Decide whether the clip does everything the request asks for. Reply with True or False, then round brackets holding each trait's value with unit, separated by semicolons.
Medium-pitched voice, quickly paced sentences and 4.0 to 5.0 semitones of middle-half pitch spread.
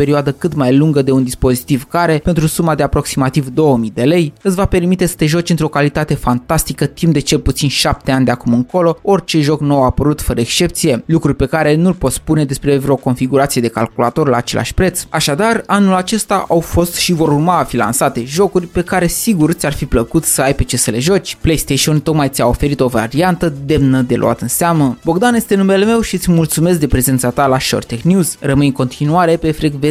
True (150 Hz; 220 wpm; 4.5 semitones)